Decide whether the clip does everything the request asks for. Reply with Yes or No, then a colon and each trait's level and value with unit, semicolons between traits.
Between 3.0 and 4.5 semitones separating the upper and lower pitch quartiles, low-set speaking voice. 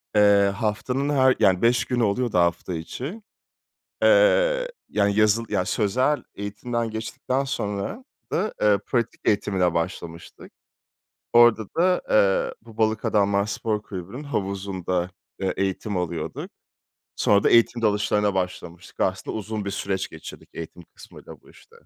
Yes: average, 3.6 semitones; low, 105 Hz